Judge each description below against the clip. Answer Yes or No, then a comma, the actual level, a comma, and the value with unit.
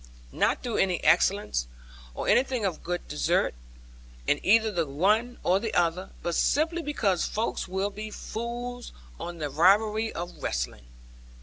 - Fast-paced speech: No, average, 145 wpm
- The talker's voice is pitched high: Yes, high, 195 Hz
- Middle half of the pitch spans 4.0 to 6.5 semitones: Yes, average, 4.8 semitones